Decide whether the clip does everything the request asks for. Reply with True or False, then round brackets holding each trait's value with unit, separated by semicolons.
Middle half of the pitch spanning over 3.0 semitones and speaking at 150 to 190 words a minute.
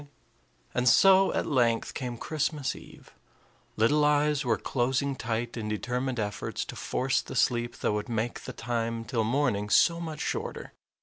True (3.9 semitones; 160 wpm)